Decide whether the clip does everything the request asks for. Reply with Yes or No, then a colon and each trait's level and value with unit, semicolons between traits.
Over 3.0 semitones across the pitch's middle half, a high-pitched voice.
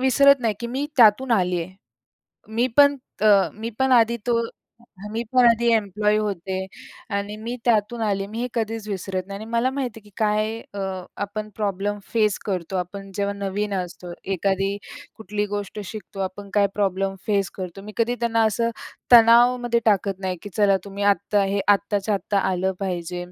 No: average, 2.7 semitones; high, 210 Hz